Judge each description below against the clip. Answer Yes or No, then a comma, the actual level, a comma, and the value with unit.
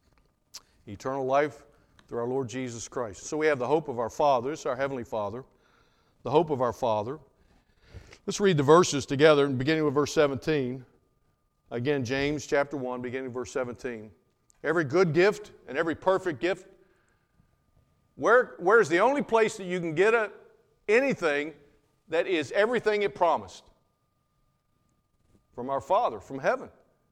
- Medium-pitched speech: Yes, medium, 145 Hz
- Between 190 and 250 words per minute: No, average, 155 wpm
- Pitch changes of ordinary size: No, wide, 6.4 semitones